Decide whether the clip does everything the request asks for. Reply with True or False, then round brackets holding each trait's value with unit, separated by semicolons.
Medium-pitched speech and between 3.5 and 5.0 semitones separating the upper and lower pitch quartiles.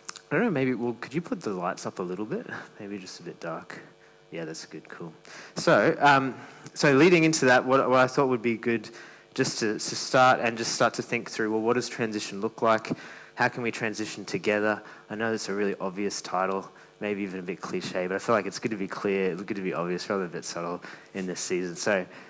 False (110 Hz; 4.2 semitones)